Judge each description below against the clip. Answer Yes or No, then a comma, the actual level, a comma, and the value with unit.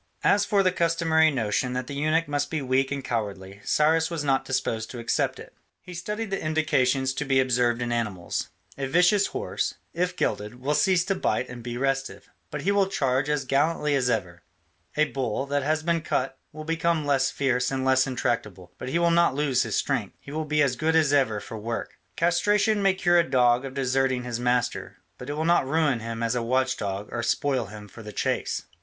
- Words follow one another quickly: Yes, fast, 215 wpm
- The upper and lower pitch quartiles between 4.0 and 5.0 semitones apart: Yes, average, 4.6 semitones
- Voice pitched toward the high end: No, low, 135 Hz